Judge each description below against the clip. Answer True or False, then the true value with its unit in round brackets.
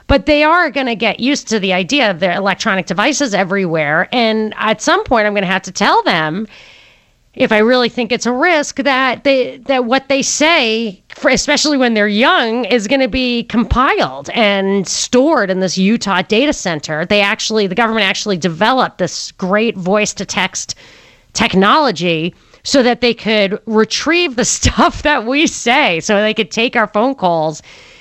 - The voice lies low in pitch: False (220 Hz)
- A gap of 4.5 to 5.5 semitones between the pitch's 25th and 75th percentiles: True (4.8 semitones)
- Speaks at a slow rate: False (180 wpm)